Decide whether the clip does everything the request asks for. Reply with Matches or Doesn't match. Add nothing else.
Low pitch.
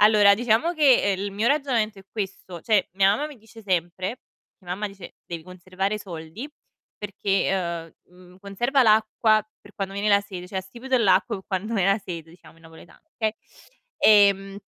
Doesn't match